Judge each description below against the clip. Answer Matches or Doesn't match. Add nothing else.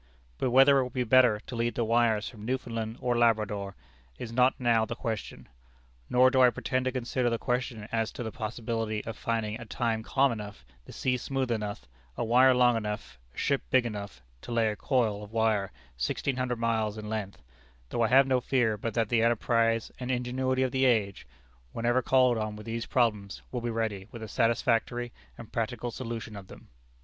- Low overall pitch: Matches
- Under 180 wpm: Doesn't match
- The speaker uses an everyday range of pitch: Doesn't match